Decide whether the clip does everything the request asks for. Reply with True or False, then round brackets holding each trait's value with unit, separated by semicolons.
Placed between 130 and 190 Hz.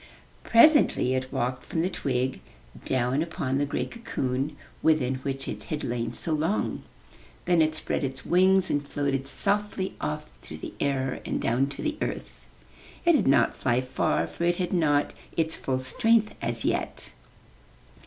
True (140 Hz)